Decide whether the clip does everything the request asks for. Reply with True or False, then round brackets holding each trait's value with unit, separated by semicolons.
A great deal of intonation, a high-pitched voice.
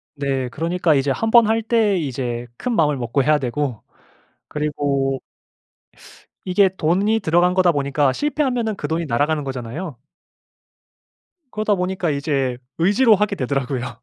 False (6.2 semitones; 150 Hz)